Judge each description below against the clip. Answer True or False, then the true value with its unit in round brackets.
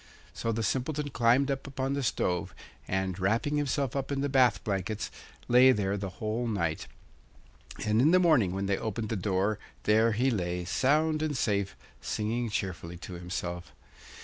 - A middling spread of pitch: False (5.7 semitones)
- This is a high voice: False (110 Hz)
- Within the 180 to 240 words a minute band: False (170 wpm)